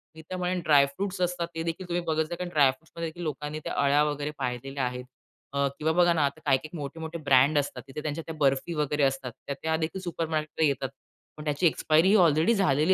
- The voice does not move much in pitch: No, average, 3.1 semitones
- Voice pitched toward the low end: No, medium, 155 Hz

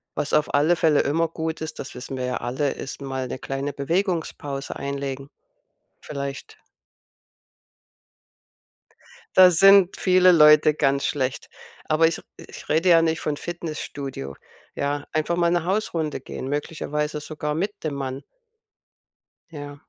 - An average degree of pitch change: Yes, average, 3.0 semitones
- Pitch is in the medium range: Yes, medium, 150 Hz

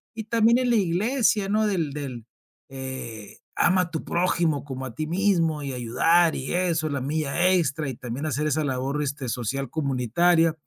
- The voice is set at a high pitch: No, medium, 155 Hz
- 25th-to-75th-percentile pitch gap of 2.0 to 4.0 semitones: No, average, 4.9 semitones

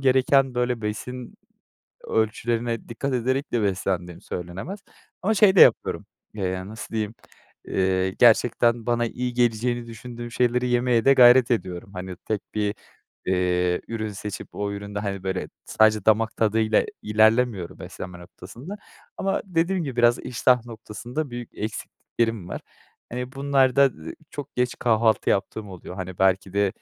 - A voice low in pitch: Yes, low, 115 Hz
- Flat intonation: No, average, 3.7 semitones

